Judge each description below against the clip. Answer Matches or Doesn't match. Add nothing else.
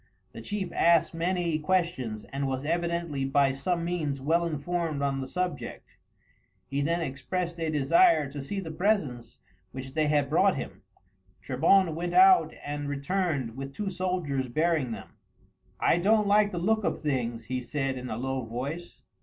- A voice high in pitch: Doesn't match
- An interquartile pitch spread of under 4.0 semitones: Doesn't match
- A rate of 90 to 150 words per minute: Doesn't match